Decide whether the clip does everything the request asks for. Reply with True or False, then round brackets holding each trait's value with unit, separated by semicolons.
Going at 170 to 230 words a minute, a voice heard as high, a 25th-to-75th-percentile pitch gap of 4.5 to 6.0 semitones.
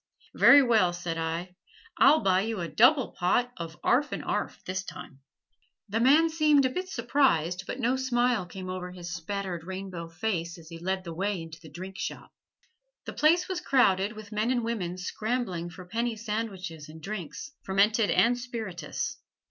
True (175 wpm; 195 Hz; 5.5 semitones)